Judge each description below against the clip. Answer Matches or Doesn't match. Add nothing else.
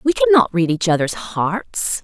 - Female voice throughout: Matches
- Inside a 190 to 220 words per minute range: Matches